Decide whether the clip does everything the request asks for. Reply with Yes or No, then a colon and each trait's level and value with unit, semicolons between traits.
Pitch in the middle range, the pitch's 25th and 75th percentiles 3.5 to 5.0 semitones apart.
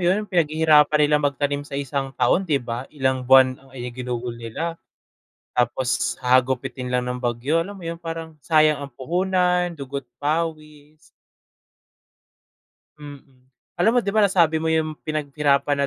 Yes: medium, 145 Hz; average, 3.9 semitones